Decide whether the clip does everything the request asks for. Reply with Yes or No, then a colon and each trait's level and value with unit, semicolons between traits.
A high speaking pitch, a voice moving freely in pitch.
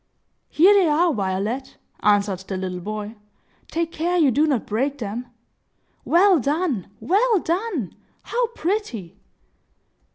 Yes: very high, 280 Hz; wide, 9.0 semitones